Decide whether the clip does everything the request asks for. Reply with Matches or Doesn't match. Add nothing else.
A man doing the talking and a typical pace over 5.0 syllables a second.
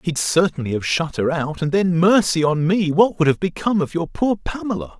Matches